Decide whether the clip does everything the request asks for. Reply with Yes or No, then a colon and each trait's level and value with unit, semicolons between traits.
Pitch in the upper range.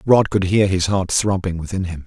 No: very low, 95 Hz